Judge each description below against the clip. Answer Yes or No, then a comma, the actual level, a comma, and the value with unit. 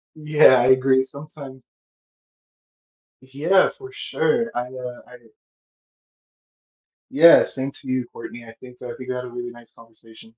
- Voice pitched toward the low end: Yes, low, 130 Hz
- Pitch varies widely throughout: No, narrow, 2.6 semitones